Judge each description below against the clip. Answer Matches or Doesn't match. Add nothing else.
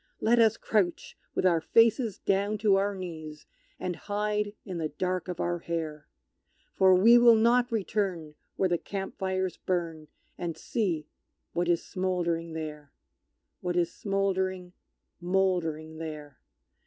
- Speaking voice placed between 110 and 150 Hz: Doesn't match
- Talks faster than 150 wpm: Doesn't match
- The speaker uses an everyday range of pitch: Matches